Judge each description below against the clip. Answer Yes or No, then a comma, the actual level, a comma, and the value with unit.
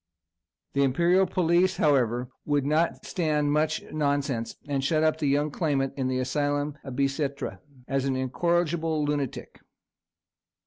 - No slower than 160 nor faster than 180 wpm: No, slow, 135 wpm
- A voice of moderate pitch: Yes, medium, 145 Hz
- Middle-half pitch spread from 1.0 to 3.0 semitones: Yes, narrow, 2.6 semitones